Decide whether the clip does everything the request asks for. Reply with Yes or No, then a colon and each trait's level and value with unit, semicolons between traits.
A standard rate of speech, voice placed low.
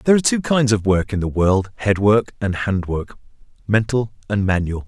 Yes: average, 195 wpm; low, 105 Hz